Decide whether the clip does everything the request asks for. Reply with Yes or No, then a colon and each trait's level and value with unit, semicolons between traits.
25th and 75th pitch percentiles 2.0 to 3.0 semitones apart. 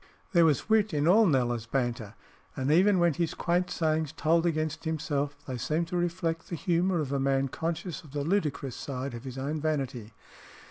No: average, 4.0 semitones